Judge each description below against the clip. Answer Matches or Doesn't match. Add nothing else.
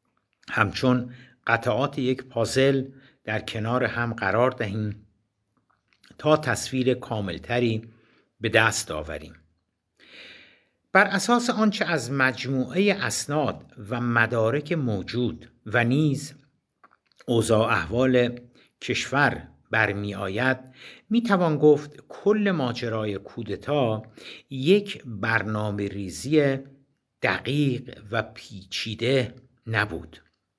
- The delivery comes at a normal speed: Doesn't match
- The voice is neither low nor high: Doesn't match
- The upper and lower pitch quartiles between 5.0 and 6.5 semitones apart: Doesn't match